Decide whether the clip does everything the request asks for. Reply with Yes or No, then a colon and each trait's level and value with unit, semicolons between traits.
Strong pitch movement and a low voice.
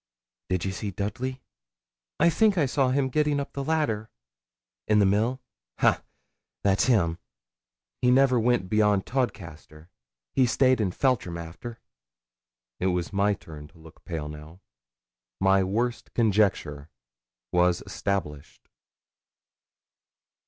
Yes: wide, 6.3 semitones; low, 105 Hz